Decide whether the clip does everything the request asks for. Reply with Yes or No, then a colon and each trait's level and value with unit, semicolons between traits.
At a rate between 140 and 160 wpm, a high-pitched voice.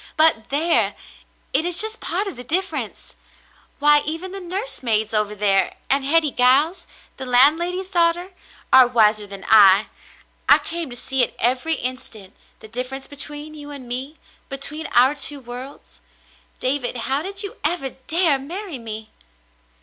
Yes: average, 155 wpm; very high, 280 Hz